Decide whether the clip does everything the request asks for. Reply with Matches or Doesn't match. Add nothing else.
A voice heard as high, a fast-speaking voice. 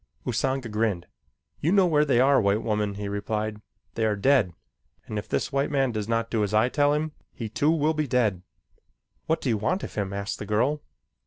Doesn't match